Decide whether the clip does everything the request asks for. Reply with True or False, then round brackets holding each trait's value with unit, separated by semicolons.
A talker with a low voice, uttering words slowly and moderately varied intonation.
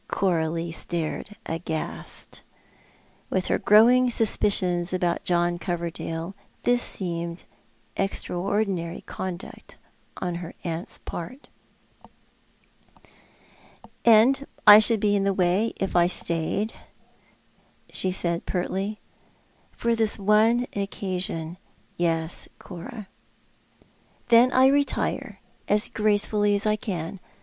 False (190 Hz; 100 wpm; 3.8 semitones)